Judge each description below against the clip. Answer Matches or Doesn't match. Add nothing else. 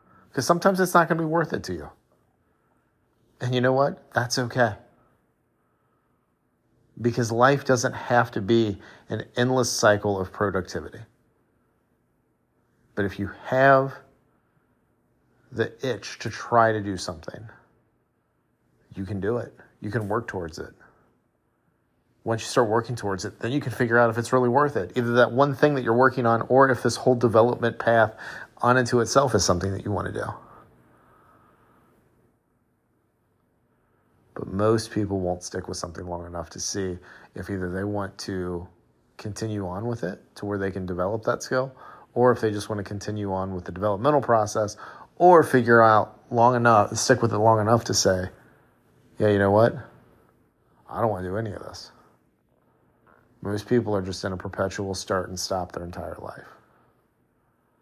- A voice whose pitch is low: Matches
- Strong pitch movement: Doesn't match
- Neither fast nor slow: Matches